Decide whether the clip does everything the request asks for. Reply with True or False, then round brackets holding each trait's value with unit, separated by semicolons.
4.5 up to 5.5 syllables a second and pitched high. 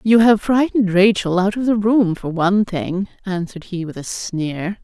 True (4.8 syllables/s; 195 Hz)